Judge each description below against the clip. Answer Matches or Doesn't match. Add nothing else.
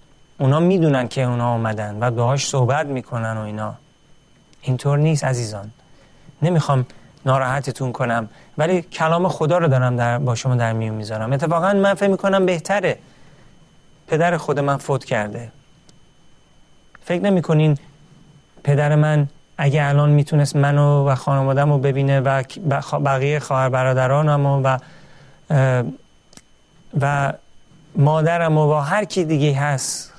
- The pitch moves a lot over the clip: Doesn't match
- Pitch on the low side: Doesn't match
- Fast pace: Doesn't match